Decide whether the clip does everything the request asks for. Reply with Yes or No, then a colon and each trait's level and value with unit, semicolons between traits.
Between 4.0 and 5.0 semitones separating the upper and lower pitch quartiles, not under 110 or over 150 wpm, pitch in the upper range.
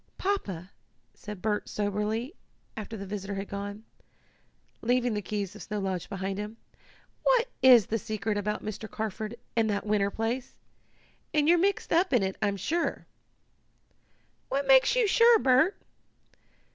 Yes: average, 4.5 semitones; average, 145 wpm; high, 215 Hz